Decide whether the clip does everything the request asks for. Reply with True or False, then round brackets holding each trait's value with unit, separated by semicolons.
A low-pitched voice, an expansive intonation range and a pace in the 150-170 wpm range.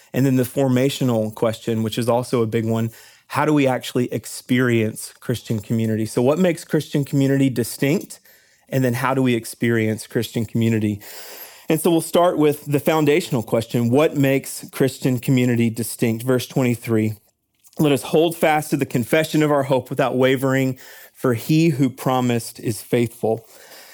False (130 Hz; 3.6 semitones; 165 wpm)